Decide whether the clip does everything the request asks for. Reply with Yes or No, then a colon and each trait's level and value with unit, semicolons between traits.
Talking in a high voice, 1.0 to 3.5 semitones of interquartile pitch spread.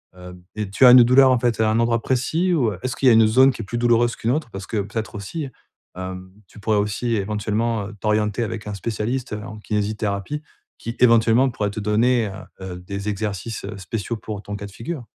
No: low, 110 Hz; average, 2.8 semitones